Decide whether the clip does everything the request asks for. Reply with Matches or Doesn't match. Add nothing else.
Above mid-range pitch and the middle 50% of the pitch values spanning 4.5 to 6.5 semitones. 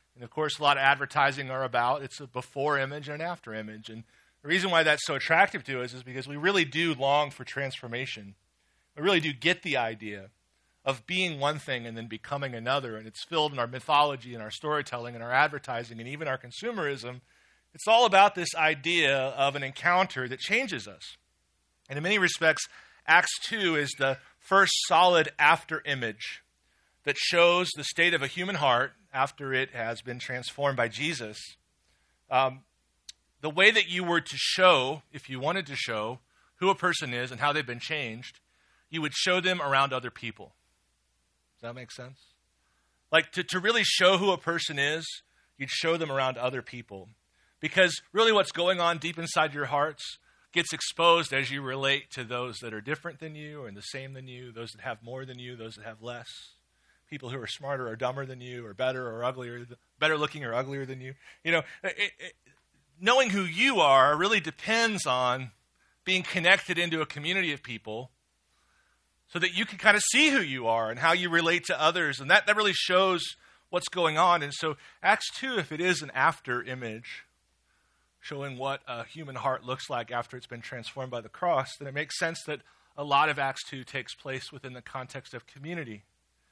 Doesn't match